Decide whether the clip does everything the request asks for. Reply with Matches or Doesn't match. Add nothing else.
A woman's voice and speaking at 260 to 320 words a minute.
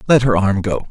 Doesn't match